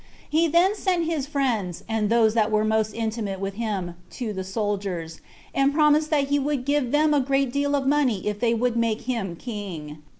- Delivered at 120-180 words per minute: No, average, 200 wpm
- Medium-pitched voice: No, high, 235 Hz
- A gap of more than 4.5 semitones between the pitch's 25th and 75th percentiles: Yes, wide, 5.6 semitones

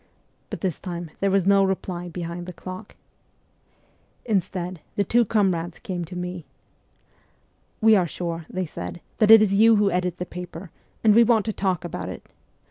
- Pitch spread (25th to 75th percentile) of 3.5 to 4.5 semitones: No, average, 2.7 semitones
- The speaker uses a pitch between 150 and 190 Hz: Yes, medium, 185 Hz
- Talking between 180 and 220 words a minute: Yes, average, 185 wpm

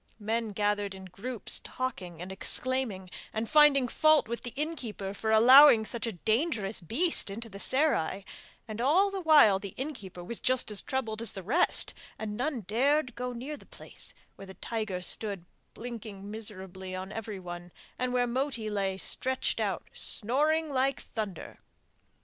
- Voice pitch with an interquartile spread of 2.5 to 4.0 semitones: No, average, 4.8 semitones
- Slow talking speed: No, average, 160 wpm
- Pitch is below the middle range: No, high, 225 Hz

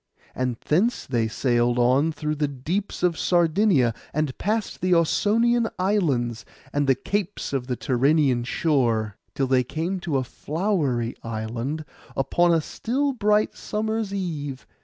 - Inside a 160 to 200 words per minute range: No, average, 140 wpm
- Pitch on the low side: No, medium, 150 Hz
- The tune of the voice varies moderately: No, wide, 7.2 semitones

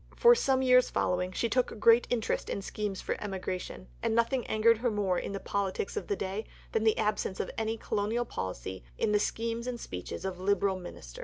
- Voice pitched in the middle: No, high, 210 Hz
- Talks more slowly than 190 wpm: No, fast, 205 wpm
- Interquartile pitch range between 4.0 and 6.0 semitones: No, average, 3.4 semitones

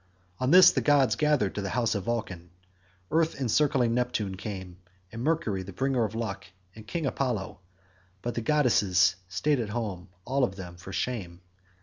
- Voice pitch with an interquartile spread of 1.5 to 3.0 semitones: No, wide, 5.4 semitones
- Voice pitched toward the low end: Yes, low, 115 Hz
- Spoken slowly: No, average, 175 wpm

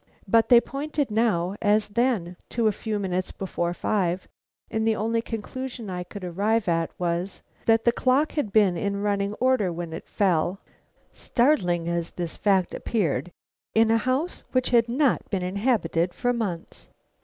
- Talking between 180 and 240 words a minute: No, average, 165 wpm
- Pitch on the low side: No, high, 205 Hz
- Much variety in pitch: No, average, 4.6 semitones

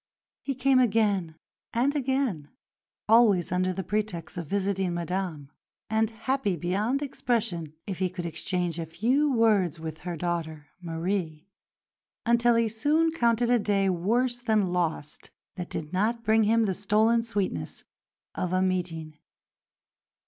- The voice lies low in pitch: No, high, 195 Hz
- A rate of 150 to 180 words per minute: No, average, 140 wpm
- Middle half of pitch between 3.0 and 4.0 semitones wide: No, average, 5.0 semitones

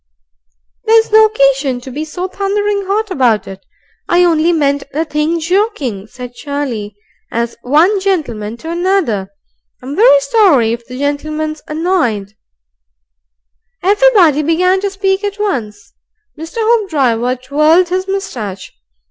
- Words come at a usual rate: No, slow, 130 wpm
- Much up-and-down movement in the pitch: Yes, wide, 7.7 semitones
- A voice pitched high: Yes, very high, 310 Hz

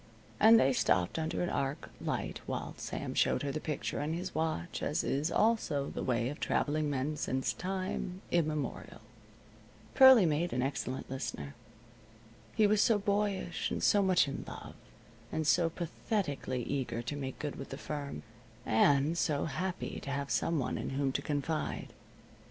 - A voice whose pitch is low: No, medium, 150 Hz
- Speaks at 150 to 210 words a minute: Yes, average, 165 wpm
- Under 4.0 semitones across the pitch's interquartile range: No, average, 4.4 semitones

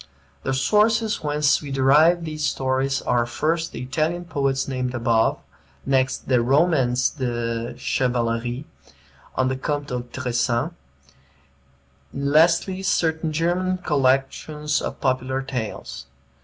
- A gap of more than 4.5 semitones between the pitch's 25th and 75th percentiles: No, average, 3.8 semitones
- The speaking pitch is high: No, low, 135 Hz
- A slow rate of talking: Yes, slow, 115 wpm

